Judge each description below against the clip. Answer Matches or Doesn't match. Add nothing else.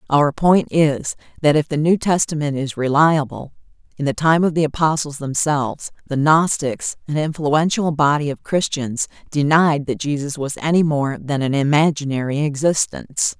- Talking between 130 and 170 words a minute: Matches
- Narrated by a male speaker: Doesn't match